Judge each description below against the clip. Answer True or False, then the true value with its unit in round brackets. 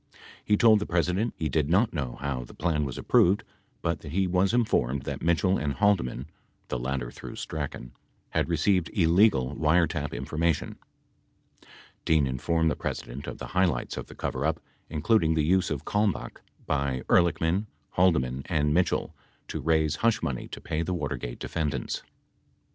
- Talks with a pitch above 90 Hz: False (80 Hz)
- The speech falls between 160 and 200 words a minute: True (165 wpm)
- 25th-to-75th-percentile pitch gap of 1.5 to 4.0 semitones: False (4.6 semitones)